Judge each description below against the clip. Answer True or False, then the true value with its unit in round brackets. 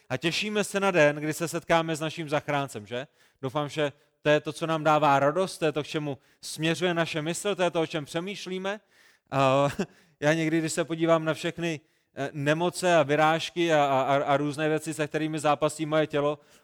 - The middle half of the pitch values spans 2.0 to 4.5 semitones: True (2.3 semitones)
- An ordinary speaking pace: False (190 wpm)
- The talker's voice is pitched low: False (155 Hz)